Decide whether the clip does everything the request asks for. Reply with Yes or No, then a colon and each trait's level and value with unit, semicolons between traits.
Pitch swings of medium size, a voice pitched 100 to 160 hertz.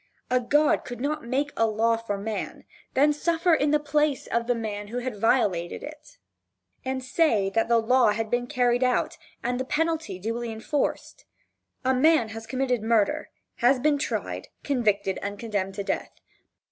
No: average, 4.5 semitones; high, 245 Hz